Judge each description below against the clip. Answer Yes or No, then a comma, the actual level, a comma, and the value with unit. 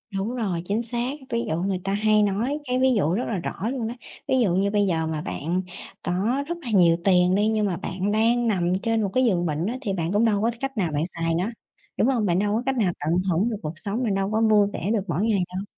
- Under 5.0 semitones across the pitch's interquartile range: Yes, average, 4.2 semitones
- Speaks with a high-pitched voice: Yes, high, 205 Hz